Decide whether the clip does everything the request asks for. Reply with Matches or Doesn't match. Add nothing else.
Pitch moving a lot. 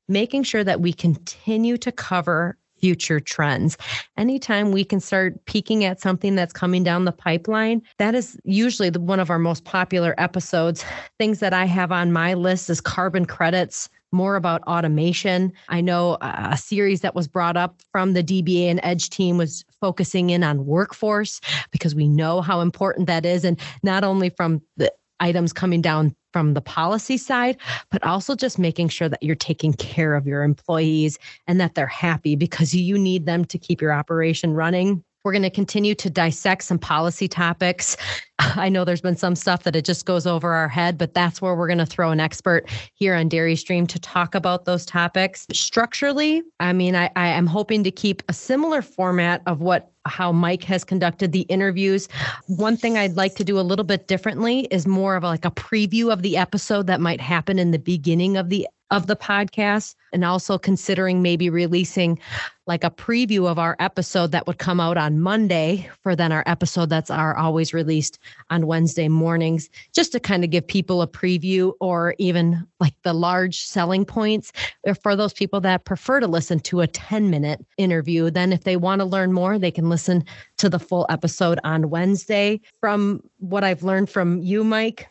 Doesn't match